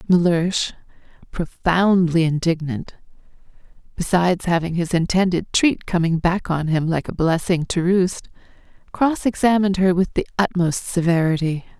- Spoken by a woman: Yes, female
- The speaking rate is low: Yes, slow, 120 wpm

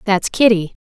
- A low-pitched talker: No, high, 200 Hz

